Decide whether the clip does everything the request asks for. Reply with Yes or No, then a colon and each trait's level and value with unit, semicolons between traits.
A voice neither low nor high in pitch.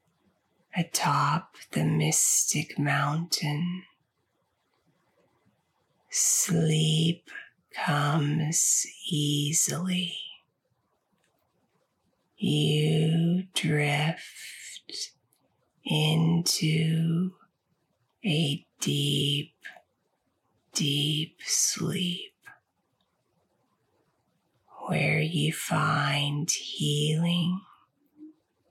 Yes: medium, 160 Hz